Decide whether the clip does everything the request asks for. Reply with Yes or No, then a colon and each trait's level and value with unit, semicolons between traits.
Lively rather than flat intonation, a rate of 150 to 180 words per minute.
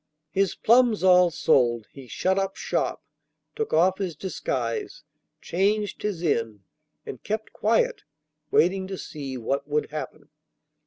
No: wide, 6.1 semitones; slow, 135 wpm